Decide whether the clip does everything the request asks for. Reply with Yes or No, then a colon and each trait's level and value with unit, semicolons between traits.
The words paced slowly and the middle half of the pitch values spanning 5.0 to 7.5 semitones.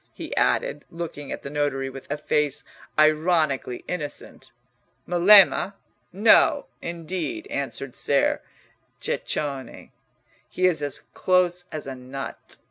No: slow, 115 wpm; average, 4.3 semitones